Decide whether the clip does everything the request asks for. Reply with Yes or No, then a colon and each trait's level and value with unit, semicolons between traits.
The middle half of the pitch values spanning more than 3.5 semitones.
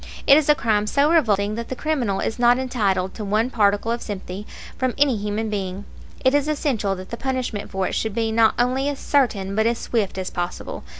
Yes: average, 4.3 semitones